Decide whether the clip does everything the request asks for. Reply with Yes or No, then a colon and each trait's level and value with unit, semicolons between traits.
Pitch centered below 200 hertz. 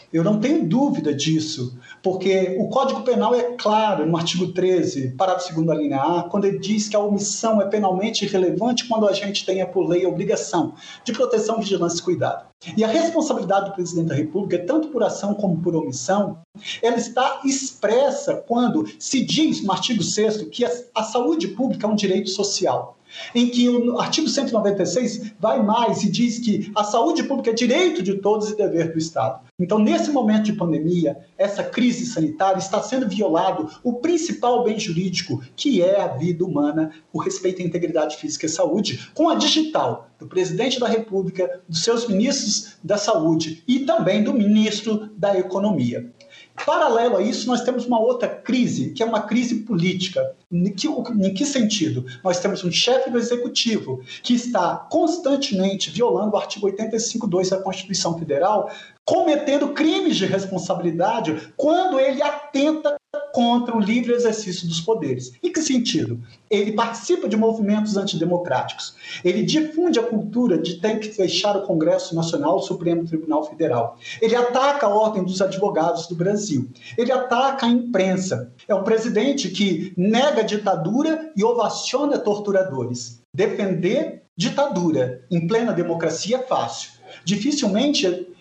No: high, 205 Hz